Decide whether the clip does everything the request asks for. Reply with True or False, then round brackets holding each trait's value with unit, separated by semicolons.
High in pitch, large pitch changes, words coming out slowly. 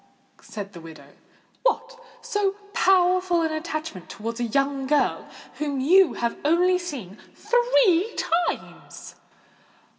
True (325 Hz; 6.0 semitones; 115 wpm)